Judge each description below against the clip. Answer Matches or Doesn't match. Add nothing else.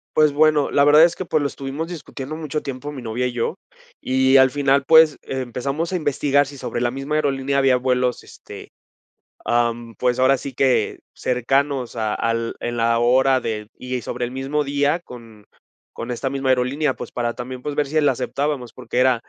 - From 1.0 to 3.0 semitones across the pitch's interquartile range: Matches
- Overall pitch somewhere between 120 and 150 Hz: Matches